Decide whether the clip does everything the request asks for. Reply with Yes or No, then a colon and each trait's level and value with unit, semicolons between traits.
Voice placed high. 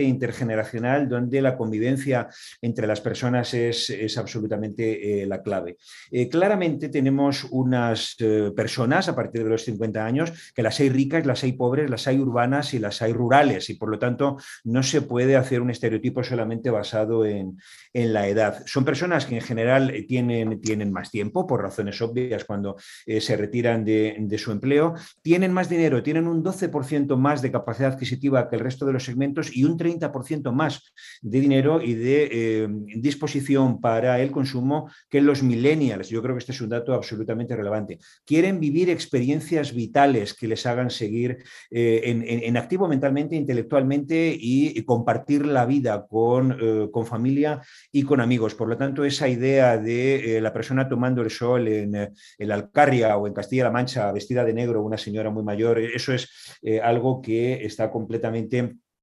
No: low, 125 Hz